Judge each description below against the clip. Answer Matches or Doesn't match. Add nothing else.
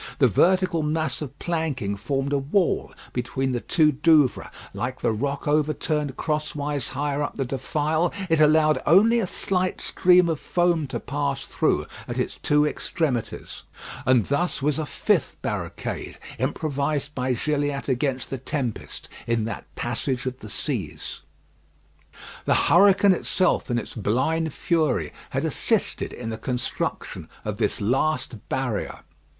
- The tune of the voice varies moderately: Matches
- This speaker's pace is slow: Doesn't match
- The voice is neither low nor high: Matches